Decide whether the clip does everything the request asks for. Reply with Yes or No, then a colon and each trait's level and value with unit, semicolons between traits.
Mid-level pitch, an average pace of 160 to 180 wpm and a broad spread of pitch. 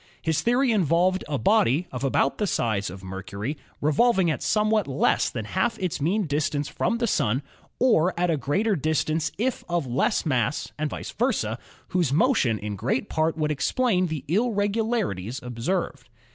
Yes: medium, 160 Hz; average, 170 wpm; wide, 7.4 semitones